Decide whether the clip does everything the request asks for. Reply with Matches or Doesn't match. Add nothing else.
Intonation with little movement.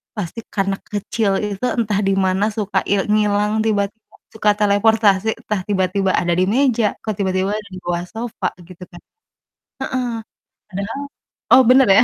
Matches